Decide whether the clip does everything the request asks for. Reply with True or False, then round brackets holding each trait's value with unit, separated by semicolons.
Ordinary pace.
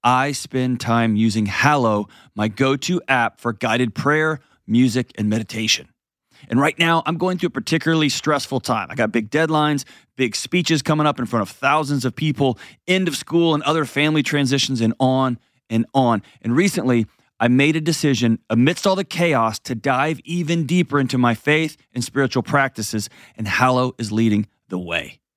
True (180 wpm)